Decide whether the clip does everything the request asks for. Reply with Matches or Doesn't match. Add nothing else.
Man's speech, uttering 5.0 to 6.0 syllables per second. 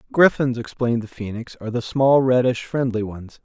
Matches